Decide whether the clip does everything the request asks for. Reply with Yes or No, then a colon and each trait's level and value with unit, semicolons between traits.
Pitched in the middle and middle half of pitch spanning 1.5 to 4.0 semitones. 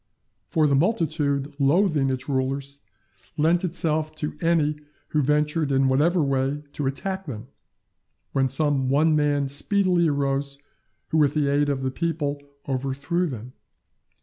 Yes: medium, 145 Hz; narrow, 2.5 semitones